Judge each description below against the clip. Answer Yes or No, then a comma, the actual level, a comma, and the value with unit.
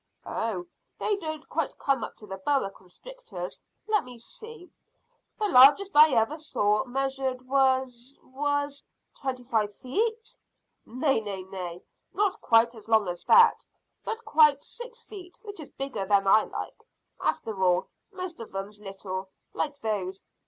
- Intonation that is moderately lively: No, wide, 7.2 semitones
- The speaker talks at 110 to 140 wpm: No, average, 150 wpm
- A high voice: Yes, very high, 260 Hz